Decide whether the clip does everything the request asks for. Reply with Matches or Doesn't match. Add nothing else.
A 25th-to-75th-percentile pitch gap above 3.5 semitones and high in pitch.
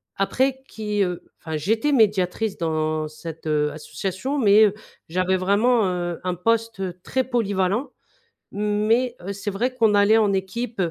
Matches